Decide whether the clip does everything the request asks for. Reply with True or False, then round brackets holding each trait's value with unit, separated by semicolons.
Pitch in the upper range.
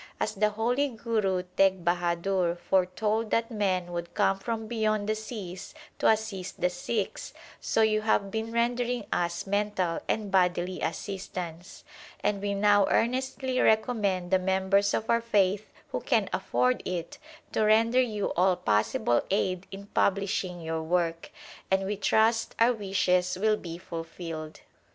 True (195 Hz)